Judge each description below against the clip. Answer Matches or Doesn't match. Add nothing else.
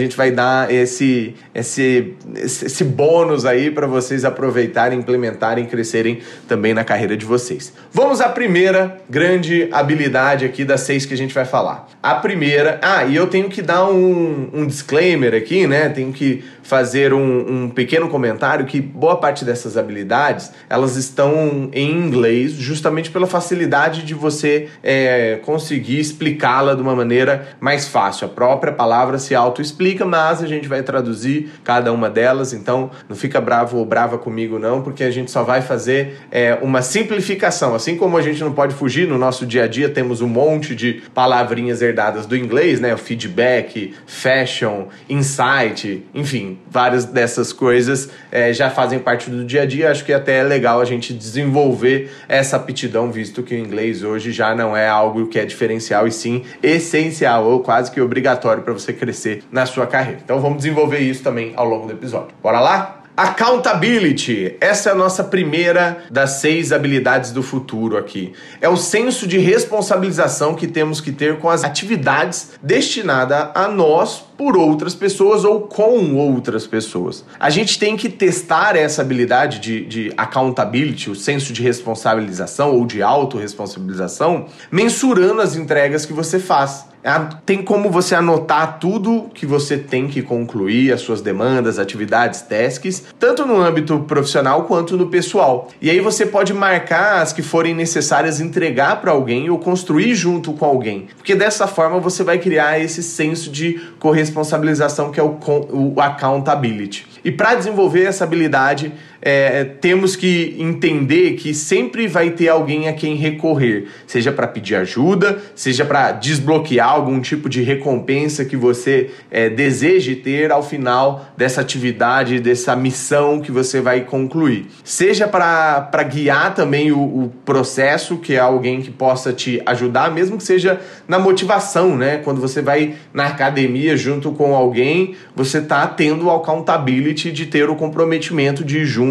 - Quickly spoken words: Doesn't match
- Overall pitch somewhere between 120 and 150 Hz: Matches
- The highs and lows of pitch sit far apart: Doesn't match